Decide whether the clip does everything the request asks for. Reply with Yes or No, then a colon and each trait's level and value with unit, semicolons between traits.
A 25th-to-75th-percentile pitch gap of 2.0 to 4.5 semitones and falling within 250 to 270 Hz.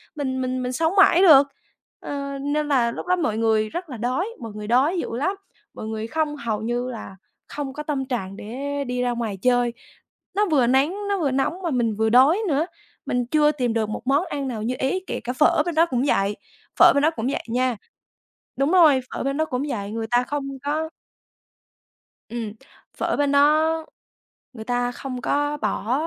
Yes: average, 3.9 semitones; very high, 265 Hz